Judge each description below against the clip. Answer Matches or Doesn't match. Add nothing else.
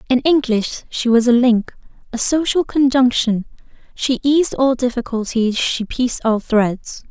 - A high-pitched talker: Matches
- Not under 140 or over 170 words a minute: Matches